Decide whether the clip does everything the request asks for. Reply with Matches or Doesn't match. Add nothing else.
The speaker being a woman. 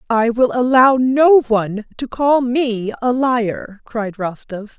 Matches